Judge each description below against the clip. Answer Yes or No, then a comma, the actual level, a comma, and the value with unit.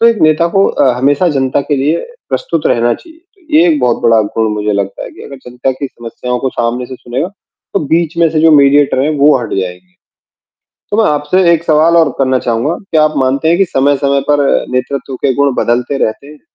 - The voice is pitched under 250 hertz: Yes, medium, 140 Hz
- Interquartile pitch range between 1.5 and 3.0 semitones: No, average, 4.5 semitones